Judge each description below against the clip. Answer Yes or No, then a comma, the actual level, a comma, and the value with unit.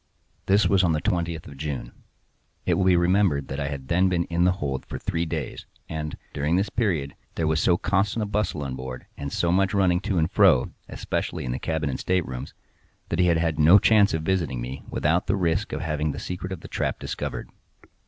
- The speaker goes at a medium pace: No, fast, 220 wpm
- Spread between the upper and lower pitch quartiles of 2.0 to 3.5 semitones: No, average, 4.0 semitones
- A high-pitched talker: No, very low, 85 Hz